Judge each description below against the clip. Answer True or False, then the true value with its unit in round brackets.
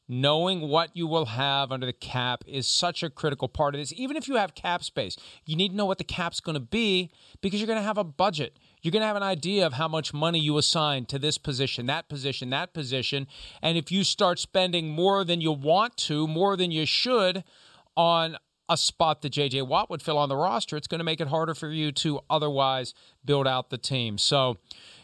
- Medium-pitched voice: True (155 Hz)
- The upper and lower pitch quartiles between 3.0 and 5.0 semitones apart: True (4.0 semitones)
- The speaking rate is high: True (235 wpm)